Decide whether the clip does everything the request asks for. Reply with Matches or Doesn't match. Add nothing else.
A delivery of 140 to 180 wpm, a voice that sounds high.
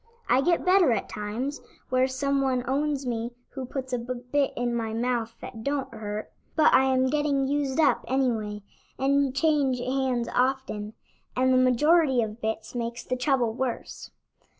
Matches